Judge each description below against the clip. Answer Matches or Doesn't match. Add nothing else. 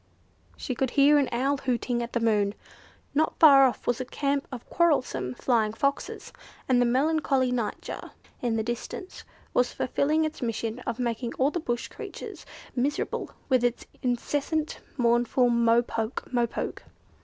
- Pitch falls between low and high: Doesn't match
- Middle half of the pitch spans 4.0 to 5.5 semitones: Doesn't match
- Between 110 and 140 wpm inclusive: Doesn't match